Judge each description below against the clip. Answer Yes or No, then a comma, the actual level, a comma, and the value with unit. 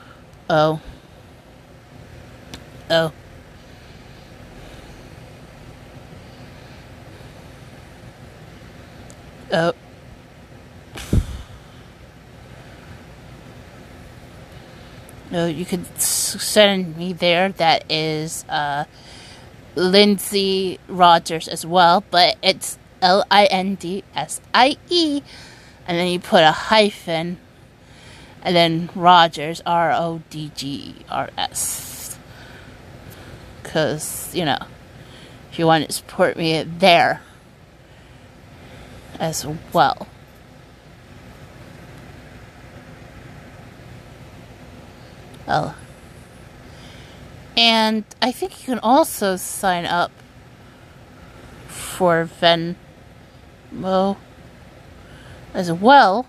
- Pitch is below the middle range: No, medium, 160 Hz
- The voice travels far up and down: Yes, wide, 6.3 semitones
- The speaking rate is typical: No, slow, 65 wpm